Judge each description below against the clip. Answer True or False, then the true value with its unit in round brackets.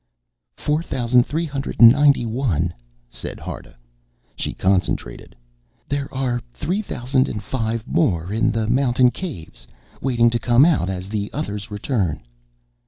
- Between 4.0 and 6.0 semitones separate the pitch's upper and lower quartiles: True (4.9 semitones)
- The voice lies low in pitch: True (120 Hz)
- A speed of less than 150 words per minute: True (140 wpm)